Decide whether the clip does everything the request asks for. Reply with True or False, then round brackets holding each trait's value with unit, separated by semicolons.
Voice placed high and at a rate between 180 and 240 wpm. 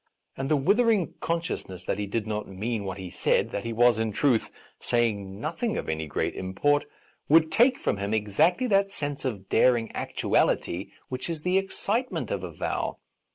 False (120 Hz; 185 wpm)